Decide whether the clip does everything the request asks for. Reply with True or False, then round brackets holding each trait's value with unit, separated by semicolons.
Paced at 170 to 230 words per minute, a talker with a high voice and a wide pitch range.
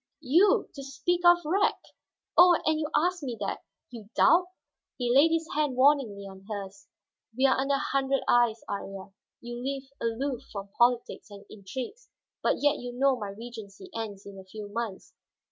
True (180 wpm; 245 Hz; 6.0 semitones)